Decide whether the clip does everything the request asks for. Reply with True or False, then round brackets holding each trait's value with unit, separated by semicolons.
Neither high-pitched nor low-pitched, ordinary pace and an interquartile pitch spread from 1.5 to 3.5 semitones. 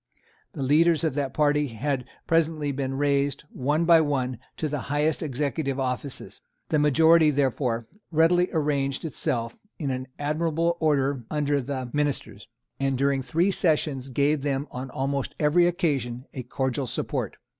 True (145 Hz; 145 wpm; 2.6 semitones)